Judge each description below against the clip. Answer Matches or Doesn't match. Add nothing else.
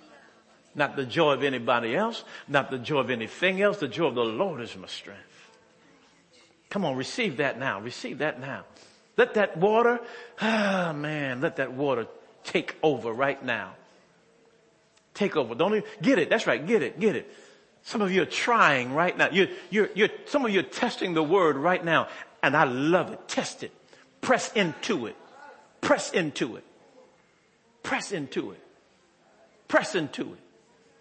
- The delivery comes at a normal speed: Matches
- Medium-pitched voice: Matches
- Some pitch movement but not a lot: Doesn't match